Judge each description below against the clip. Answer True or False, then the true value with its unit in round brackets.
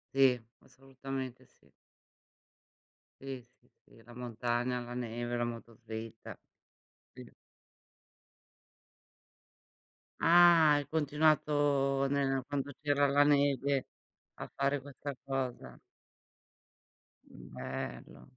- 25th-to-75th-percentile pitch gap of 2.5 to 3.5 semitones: True (2.8 semitones)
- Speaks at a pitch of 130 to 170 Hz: True (135 Hz)